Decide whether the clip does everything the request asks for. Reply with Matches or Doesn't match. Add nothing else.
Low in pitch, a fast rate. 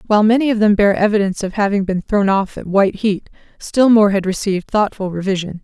Doesn't match